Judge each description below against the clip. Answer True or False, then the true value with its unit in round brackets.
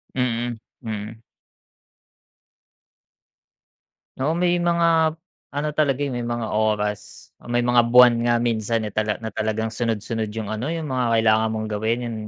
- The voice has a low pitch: True (120 Hz)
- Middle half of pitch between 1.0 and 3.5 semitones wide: True (2.9 semitones)